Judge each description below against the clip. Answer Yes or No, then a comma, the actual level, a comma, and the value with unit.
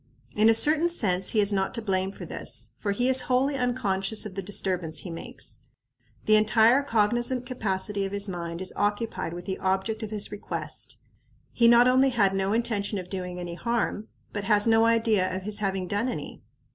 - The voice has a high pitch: Yes, high, 210 Hz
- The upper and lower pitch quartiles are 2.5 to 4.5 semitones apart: Yes, average, 3.4 semitones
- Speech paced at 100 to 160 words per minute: No, average, 195 wpm